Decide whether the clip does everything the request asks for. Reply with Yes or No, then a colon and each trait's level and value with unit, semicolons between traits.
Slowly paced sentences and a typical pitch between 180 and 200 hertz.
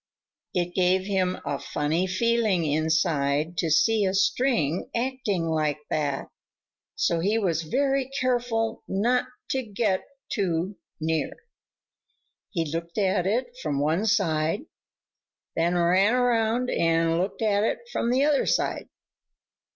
Yes: slow, 130 wpm; high, 190 Hz